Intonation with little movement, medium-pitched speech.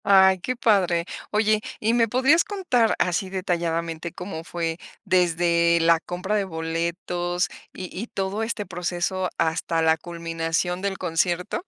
No: average, 3.1 semitones; medium, 180 Hz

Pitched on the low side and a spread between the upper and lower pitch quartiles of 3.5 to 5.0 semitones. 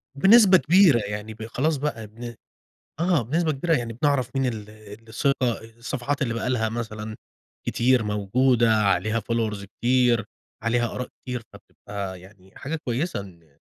Yes: low, 115 Hz; average, 3.9 semitones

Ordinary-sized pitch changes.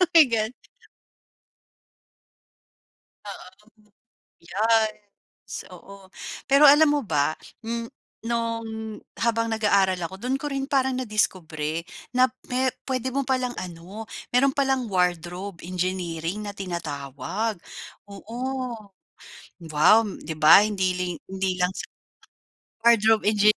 Yes: average, 4.4 semitones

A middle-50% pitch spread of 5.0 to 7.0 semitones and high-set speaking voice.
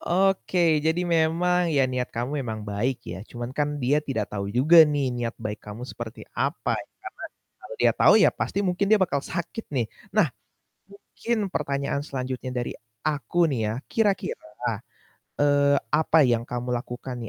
No: wide, 5.4 semitones; medium, 140 Hz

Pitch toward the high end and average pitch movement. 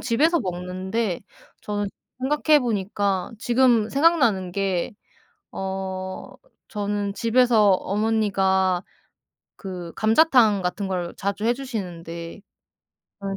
Yes: high, 200 Hz; average, 3.5 semitones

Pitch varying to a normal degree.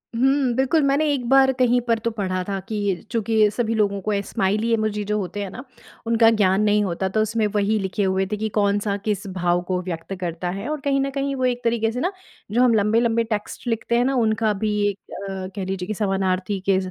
Yes: average, 3.3 semitones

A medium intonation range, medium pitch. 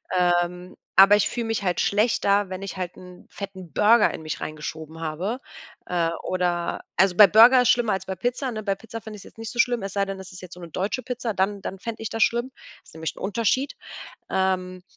No: average, 3.7 semitones; high, 195 Hz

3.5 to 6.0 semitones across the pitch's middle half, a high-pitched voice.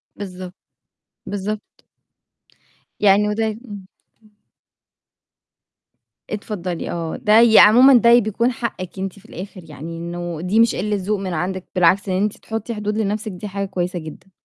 No: average, 2.8 semitones; high, 200 Hz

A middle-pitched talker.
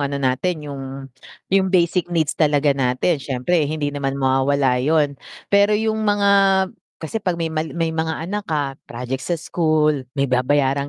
Yes: medium, 150 Hz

